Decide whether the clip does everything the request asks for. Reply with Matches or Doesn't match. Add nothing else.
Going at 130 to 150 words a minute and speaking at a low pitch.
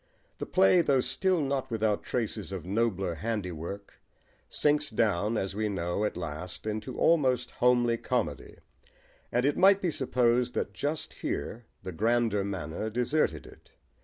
Matches